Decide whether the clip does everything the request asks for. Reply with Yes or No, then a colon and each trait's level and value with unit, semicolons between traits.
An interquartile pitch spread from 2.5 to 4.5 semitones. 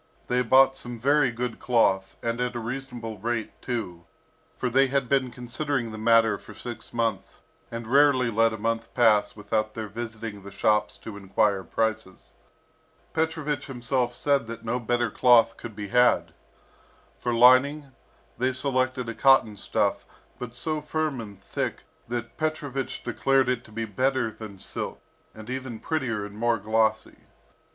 Yes: average, 2.9 semitones